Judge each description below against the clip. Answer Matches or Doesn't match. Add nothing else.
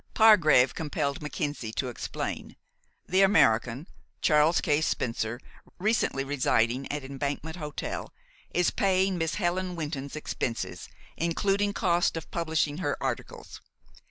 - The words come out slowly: Matches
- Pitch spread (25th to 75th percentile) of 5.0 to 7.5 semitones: Doesn't match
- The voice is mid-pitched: Matches